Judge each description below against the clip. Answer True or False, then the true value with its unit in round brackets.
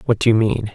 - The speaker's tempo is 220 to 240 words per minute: False (325 wpm)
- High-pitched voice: False (110 Hz)